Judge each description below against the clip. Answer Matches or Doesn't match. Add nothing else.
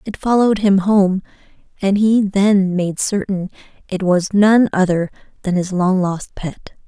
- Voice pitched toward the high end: Matches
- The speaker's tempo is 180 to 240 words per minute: Doesn't match